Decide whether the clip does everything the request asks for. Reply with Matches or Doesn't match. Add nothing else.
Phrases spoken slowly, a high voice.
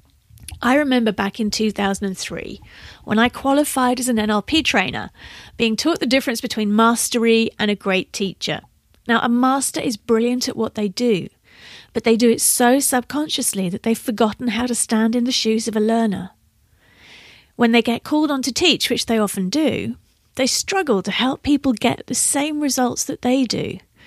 Doesn't match